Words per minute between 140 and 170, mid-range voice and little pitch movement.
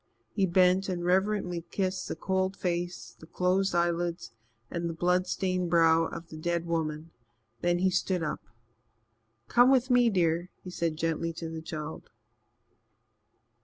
Yes: average, 150 wpm; medium, 175 Hz; narrow, 2.2 semitones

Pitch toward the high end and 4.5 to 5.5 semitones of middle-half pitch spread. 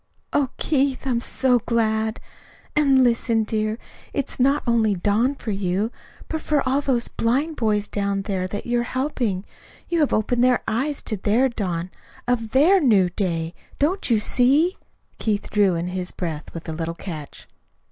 Yes: high, 230 Hz; average, 4.9 semitones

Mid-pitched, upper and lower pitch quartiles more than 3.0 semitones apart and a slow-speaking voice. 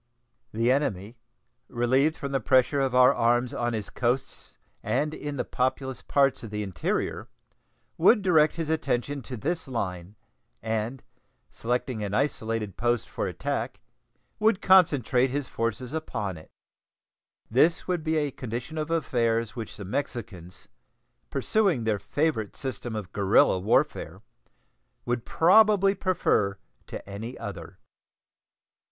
No: low, 125 Hz; average, 5.1 semitones; slow, 130 wpm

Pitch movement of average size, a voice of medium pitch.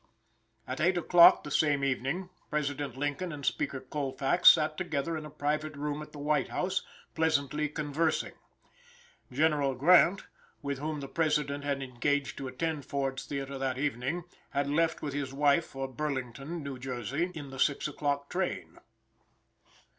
No: narrow, 2.1 semitones; medium, 145 Hz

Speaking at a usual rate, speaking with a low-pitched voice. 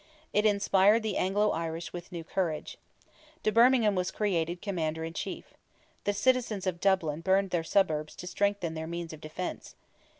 No: average, 165 wpm; medium, 185 Hz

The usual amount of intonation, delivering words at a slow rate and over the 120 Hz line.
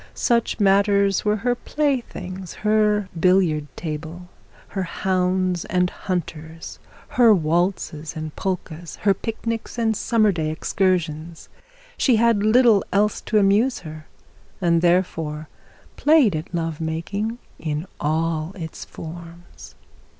Yes: average, 4.5 semitones; slow, 115 wpm; medium, 185 Hz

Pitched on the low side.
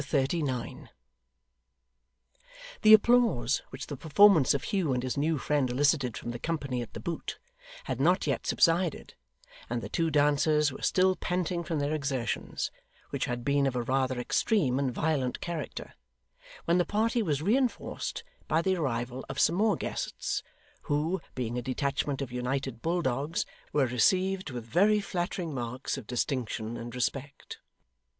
No: medium, 145 Hz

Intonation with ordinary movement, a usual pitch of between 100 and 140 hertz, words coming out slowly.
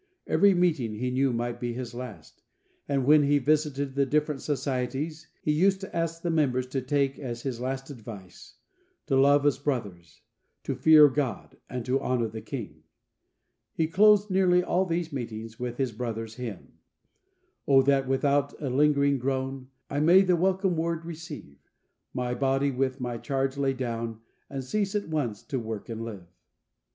No: average, 3.8 semitones; low, 135 Hz; average, 170 wpm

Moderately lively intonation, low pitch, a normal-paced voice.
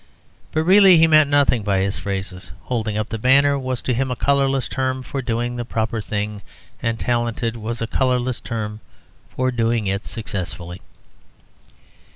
Yes: average, 3.5 semitones; low, 120 Hz; average, 165 wpm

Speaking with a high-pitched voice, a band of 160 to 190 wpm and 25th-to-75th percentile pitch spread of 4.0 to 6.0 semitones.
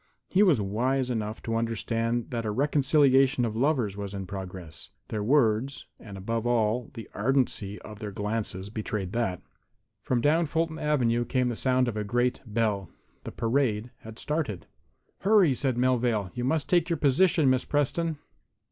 No: low, 120 Hz; average, 165 wpm; average, 4.3 semitones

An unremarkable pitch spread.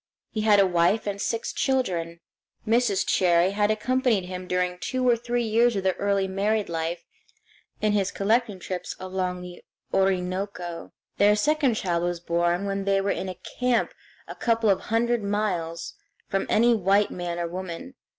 Yes: average, 3.5 semitones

